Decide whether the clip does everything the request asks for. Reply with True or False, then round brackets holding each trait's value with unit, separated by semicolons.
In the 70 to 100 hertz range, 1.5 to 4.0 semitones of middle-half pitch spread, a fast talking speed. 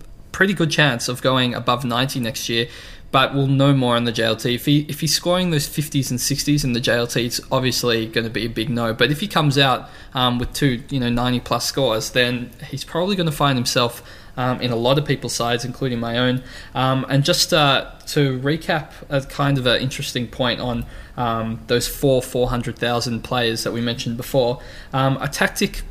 False (125 Hz; 2.9 semitones; 220 wpm)